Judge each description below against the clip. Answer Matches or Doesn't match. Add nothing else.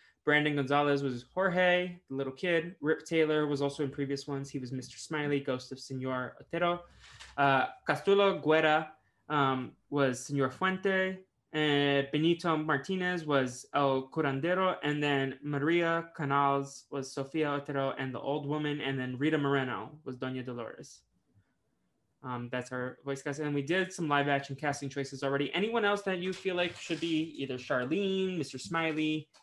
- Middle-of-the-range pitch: Matches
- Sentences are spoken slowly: Doesn't match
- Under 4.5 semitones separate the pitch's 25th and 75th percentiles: Matches